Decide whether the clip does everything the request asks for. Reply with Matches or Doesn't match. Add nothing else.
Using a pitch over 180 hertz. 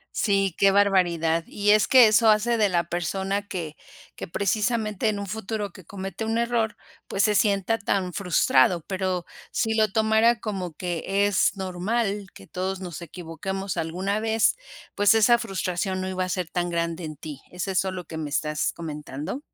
Matches